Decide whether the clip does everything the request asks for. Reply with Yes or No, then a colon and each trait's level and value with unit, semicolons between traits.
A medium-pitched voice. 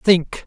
Yes: medium, 180 Hz